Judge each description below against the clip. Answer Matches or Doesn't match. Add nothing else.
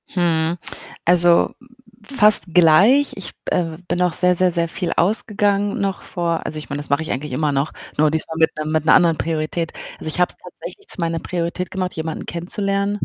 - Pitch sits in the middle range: Matches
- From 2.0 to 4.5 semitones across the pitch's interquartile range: Matches